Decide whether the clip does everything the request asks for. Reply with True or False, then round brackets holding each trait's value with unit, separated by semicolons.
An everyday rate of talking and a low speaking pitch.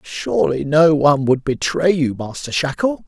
False (155 wpm; 145 Hz)